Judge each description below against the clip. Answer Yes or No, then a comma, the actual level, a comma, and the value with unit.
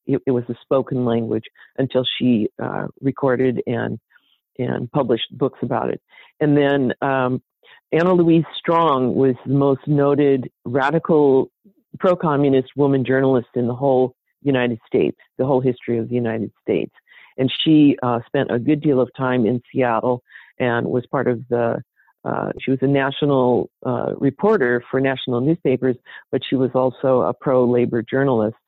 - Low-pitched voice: Yes, low, 130 Hz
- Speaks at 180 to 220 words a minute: No, average, 155 wpm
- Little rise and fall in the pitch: Yes, narrow, 2.3 semitones